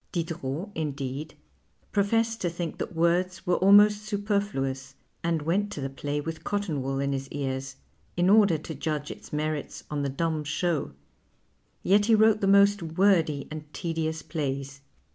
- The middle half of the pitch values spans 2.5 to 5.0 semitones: No, wide, 5.5 semitones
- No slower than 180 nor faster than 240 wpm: No, average, 160 wpm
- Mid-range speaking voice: Yes, medium, 160 Hz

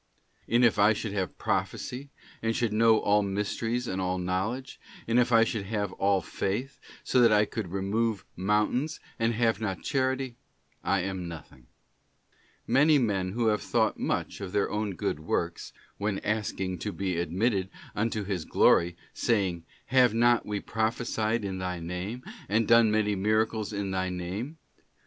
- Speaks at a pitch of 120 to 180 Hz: No, low, 105 Hz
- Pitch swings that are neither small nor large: Yes, average, 3.3 semitones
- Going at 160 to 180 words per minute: Yes, average, 165 wpm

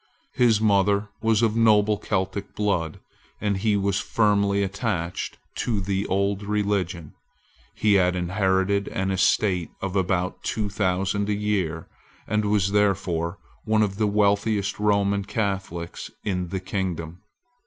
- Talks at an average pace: No, slow, 130 wpm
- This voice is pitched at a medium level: No, low, 100 Hz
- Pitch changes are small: Yes, narrow, 1.9 semitones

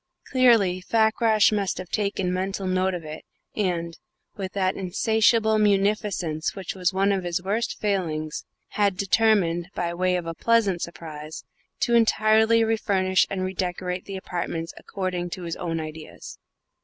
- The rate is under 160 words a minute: Yes, average, 150 wpm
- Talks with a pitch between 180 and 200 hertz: Yes, high, 190 Hz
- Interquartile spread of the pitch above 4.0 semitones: No, average, 3.2 semitones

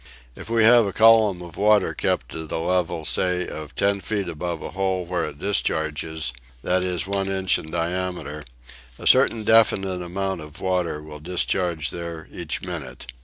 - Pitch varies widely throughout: No, average, 3.2 semitones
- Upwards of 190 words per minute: No, average, 170 wpm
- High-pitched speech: No, very low, 90 Hz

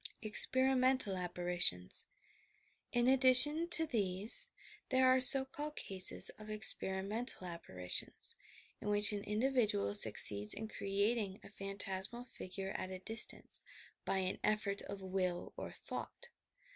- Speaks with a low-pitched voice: No, high, 205 Hz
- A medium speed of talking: No, slow, 130 wpm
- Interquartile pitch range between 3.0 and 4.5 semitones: No, average, 5.1 semitones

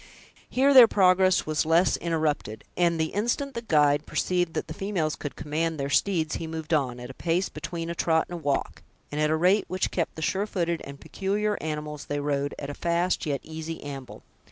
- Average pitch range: Yes, average, 3.4 semitones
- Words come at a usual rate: No, fast, 210 wpm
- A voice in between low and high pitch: Yes, medium, 160 Hz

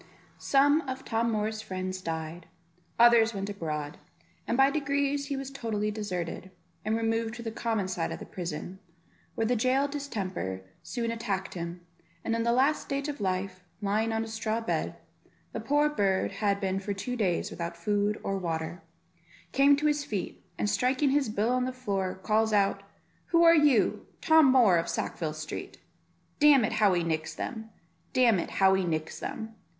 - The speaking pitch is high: Yes, high, 220 Hz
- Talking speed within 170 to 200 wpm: Yes, average, 180 wpm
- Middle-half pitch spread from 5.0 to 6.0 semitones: Yes, average, 5.3 semitones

